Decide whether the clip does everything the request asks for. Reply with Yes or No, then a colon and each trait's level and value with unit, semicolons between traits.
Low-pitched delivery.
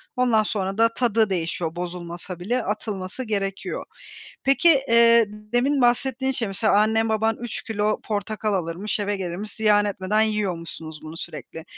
No: high, 210 Hz